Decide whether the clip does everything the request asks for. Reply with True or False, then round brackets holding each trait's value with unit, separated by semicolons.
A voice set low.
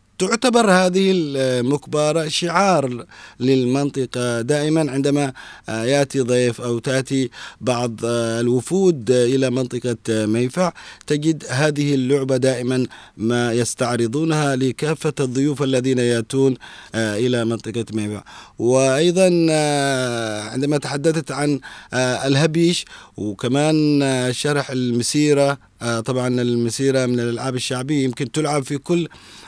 True (130 Hz)